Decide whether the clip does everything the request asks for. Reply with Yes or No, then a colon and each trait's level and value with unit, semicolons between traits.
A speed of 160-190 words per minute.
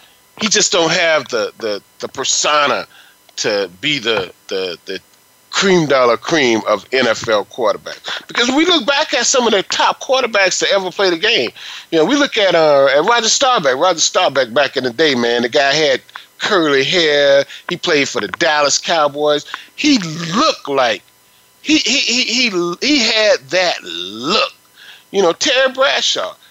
Yes: average, 170 wpm